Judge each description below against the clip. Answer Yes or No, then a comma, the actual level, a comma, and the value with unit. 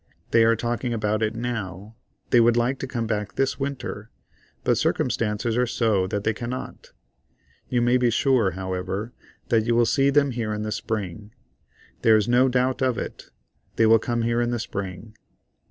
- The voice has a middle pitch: No, low, 115 Hz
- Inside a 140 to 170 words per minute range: No, average, 185 wpm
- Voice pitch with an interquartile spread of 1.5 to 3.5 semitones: Yes, narrow, 2.5 semitones